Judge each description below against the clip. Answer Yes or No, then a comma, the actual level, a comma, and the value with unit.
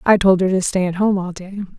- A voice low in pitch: No, high, 190 Hz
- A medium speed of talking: No, fast, 305 wpm